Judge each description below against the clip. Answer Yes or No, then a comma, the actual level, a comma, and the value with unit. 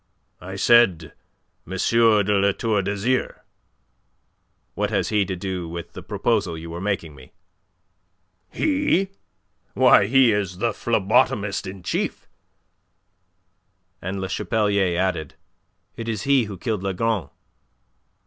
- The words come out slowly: Yes, slow, 120 wpm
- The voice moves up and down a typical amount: Yes, average, 3.6 semitones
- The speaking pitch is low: Yes, low, 100 Hz